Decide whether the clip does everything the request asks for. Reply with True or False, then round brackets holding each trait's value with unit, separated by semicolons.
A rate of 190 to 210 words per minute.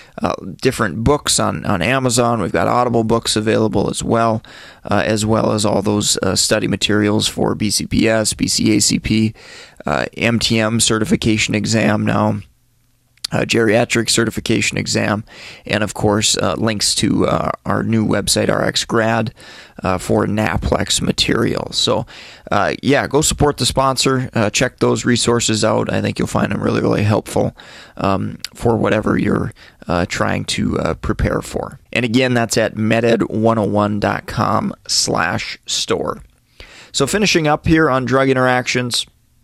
False (140 wpm)